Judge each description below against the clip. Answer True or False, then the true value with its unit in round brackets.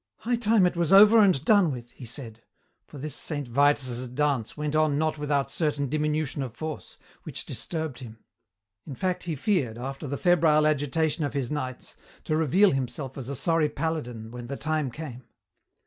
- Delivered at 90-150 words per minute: False (180 wpm)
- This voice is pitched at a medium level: True (150 Hz)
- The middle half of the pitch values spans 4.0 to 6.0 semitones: False (3.4 semitones)